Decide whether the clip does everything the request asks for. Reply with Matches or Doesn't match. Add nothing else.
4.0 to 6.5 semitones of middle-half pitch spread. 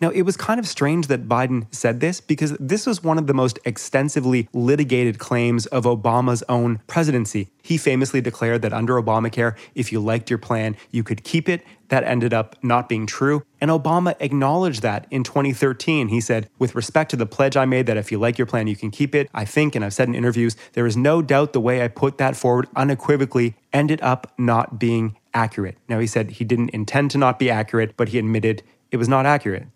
Doesn't match